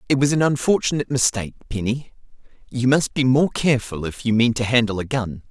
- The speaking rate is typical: Yes, average, 195 wpm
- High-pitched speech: No, low, 125 Hz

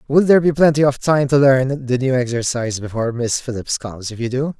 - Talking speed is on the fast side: Yes, fast, 235 wpm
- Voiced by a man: Yes, male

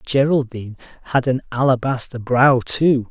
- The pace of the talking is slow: Yes, slow, 115 wpm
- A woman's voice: No, male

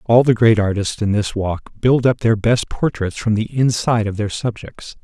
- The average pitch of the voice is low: Yes, low, 110 Hz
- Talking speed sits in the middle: No, fast, 215 wpm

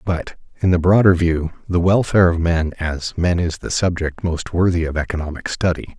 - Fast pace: No, average, 190 wpm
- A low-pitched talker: Yes, very low, 85 Hz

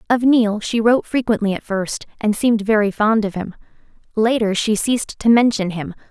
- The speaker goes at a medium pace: Yes, average, 185 wpm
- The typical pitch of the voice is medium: No, high, 215 Hz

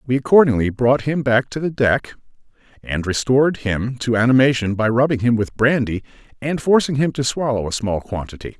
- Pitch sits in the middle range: No, low, 125 Hz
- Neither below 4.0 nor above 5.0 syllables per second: No, 5.4 syllables/s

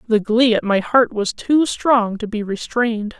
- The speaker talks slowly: No, fast, 205 wpm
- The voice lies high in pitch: Yes, high, 225 Hz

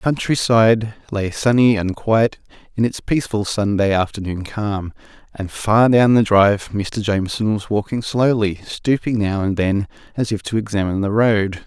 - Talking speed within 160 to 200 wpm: Yes, average, 165 wpm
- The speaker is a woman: No, male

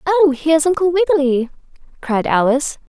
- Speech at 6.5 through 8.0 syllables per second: No, 5.6 syllables/s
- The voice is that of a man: No, female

